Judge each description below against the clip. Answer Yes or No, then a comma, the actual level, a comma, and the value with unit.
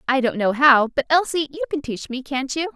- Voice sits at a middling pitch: No, very high, 270 Hz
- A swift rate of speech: Yes, fast, 260 wpm